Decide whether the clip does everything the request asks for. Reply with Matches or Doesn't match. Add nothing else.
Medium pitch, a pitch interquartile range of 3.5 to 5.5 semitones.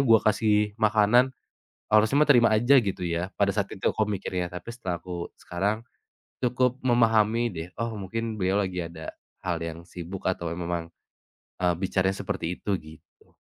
Doesn't match